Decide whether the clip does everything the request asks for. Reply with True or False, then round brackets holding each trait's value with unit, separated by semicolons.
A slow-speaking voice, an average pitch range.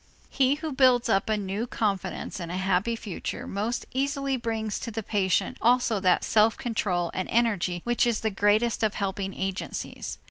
False (175 wpm; 3.7 semitones)